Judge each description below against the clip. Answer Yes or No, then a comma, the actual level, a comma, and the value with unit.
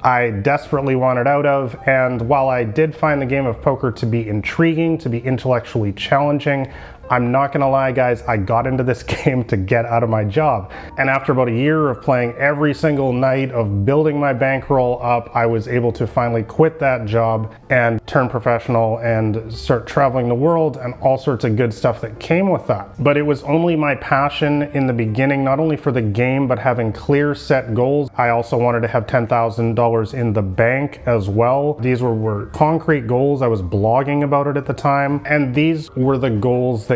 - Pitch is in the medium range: No, low, 130 Hz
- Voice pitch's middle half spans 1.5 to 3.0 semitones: No, average, 3.4 semitones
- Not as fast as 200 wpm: No, fast, 205 wpm